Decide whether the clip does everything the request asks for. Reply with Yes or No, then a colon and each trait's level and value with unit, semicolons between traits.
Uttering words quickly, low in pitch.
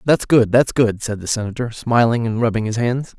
Yes: fast, 225 wpm; low, 115 Hz